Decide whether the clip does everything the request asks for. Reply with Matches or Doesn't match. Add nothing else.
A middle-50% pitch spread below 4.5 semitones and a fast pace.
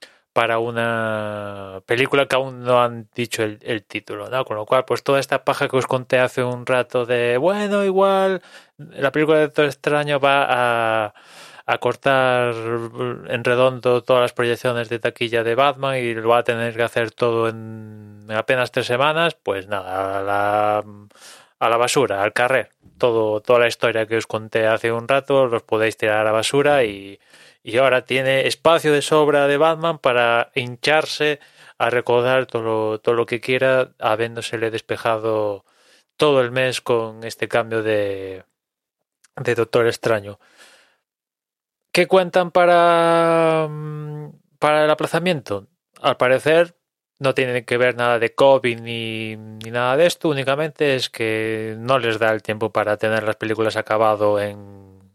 Doesn't match